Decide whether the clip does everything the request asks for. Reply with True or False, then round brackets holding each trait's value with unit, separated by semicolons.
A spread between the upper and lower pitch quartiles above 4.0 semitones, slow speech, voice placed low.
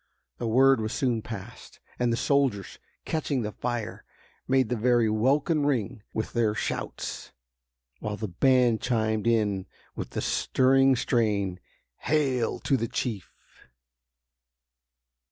False (3.4 semitones; 125 wpm; 120 Hz)